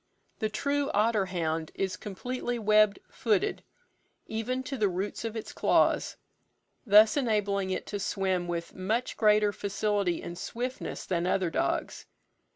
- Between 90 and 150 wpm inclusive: Yes, average, 140 wpm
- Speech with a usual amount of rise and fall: Yes, average, 3.1 semitones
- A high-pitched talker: Yes, high, 210 Hz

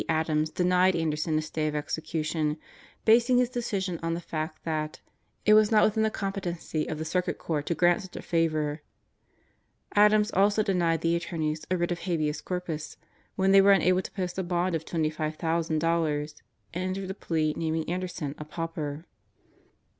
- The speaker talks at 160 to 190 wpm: Yes, average, 170 wpm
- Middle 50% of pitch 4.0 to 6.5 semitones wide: No, average, 3.2 semitones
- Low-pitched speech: No, medium, 170 Hz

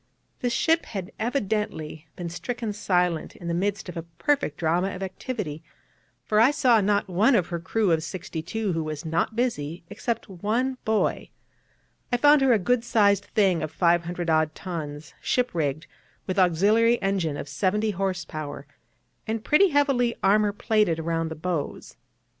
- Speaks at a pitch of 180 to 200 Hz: Yes, high, 190 Hz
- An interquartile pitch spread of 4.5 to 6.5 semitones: Yes, average, 5.2 semitones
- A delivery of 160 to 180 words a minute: Yes, average, 165 wpm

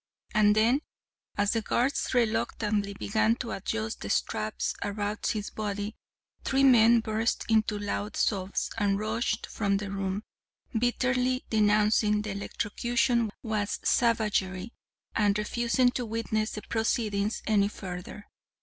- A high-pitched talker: Yes, high, 215 Hz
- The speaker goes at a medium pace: No, slow, 125 wpm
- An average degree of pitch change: No, narrow, 2.2 semitones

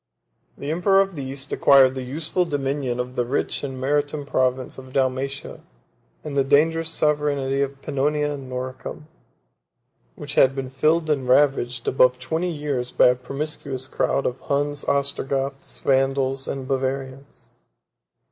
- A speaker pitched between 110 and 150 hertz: Yes, low, 135 Hz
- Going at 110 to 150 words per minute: Yes, average, 145 wpm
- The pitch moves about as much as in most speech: No, narrow, 1.9 semitones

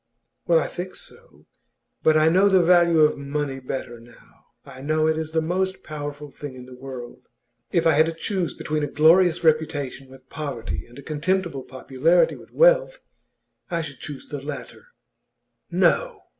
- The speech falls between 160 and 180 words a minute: Yes, average, 170 wpm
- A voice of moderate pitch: Yes, medium, 155 Hz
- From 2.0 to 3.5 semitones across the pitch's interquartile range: No, average, 4.0 semitones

